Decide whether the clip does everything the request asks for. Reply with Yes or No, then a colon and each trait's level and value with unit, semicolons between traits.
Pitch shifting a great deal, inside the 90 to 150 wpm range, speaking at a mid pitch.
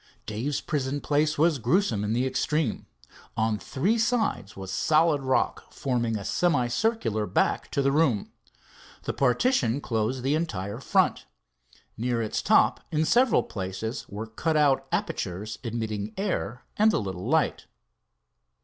No: wide, 6.1 semitones; average, 140 wpm; low, 130 Hz